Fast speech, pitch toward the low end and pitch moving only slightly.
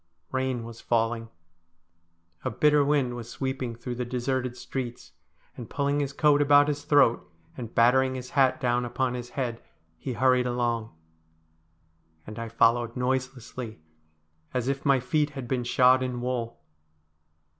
No: average, 145 wpm; low, 125 Hz; narrow, 2.0 semitones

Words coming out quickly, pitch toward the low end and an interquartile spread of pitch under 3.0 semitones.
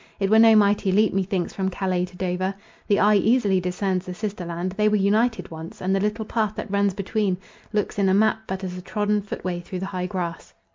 No: fast, 225 wpm; high, 195 Hz; narrow, 2.4 semitones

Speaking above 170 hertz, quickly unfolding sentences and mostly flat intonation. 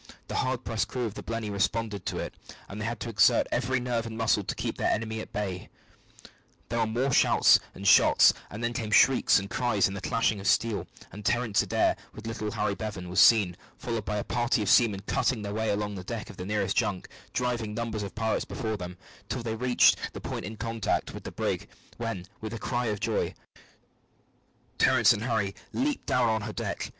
No: low, 110 Hz; fast, 215 wpm; narrow, 2.3 semitones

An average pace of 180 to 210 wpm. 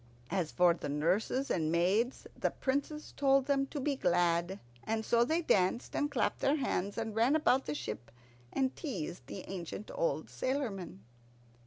No: average, 165 wpm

